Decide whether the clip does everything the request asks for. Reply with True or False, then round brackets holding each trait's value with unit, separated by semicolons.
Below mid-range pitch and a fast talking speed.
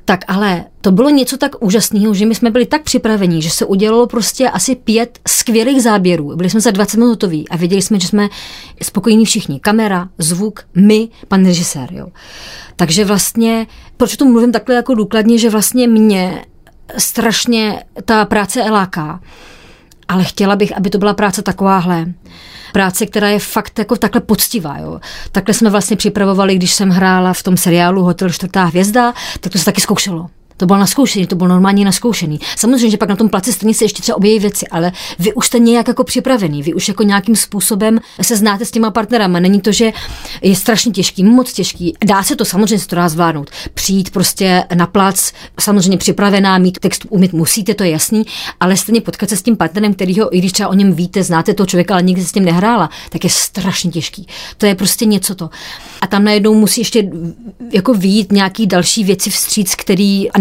False (205 Hz; 195 wpm)